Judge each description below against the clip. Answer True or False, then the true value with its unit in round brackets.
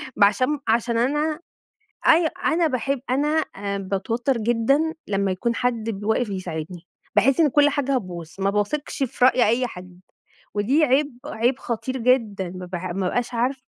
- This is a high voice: True (235 Hz)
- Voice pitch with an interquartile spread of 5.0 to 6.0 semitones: True (5.4 semitones)